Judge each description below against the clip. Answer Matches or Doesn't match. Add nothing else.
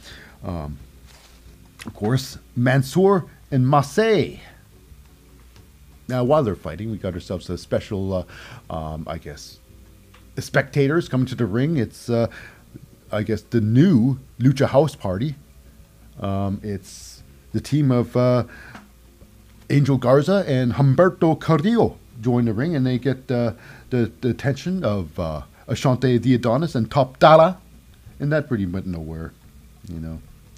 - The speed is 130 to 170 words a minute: Matches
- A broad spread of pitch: Matches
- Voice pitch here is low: Matches